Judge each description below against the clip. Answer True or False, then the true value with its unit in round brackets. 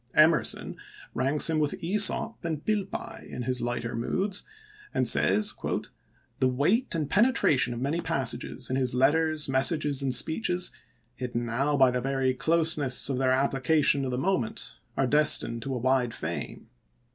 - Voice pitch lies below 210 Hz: True (135 Hz)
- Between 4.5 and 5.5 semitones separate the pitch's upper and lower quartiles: False (4.1 semitones)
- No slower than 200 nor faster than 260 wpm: False (155 wpm)